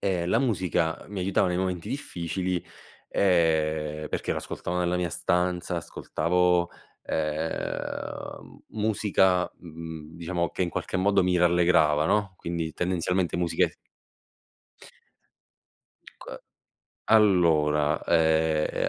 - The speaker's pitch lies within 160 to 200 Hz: No, very low, 90 Hz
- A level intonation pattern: Yes, narrow, 2.3 semitones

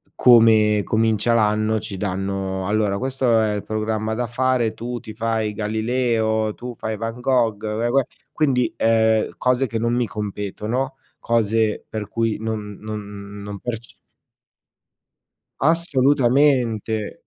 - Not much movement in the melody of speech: Yes, narrow, 2.3 semitones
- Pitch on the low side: Yes, low, 110 Hz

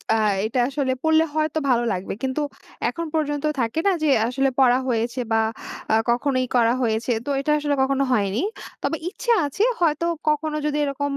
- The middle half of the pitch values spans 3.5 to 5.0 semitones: Yes, average, 3.9 semitones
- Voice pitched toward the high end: Yes, very high, 275 Hz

